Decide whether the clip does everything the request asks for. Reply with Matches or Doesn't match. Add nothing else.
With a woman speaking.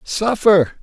Doesn't match